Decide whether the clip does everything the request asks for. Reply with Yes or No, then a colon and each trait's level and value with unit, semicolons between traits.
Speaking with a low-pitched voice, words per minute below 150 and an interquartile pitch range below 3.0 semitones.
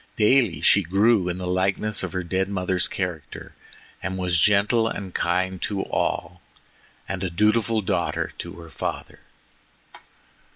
Yes: very low, 95 Hz; average, 140 wpm; narrow, 2.5 semitones